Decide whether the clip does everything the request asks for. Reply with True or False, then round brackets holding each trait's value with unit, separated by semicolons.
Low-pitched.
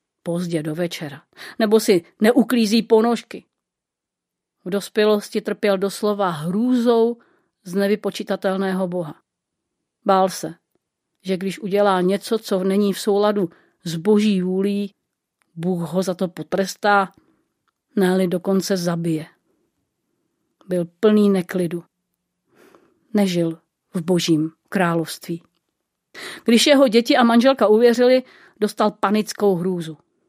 False (195 Hz)